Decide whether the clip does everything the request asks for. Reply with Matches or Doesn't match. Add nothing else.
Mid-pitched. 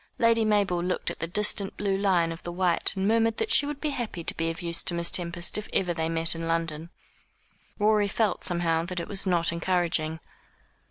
Matches